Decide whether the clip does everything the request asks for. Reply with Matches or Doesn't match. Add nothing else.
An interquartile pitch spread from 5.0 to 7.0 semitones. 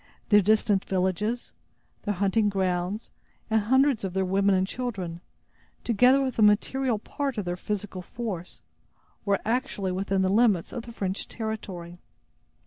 Doesn't match